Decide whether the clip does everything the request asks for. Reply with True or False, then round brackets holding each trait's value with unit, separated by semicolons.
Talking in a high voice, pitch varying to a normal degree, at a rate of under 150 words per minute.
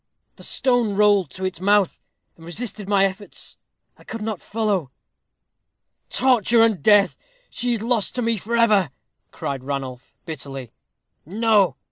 True (205 Hz; 4.5 semitones; 140 wpm)